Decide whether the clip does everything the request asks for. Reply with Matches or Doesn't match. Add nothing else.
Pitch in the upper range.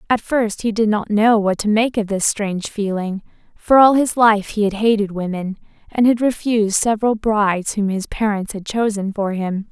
Matches